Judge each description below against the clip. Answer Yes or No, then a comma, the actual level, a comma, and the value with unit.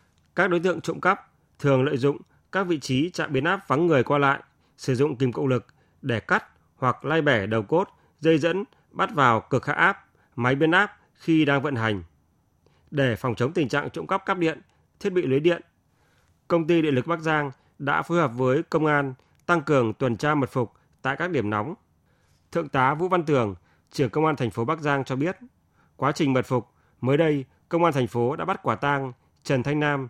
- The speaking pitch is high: No, medium, 140 Hz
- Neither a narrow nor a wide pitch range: Yes, average, 4.5 semitones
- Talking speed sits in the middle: Yes, average, 220 wpm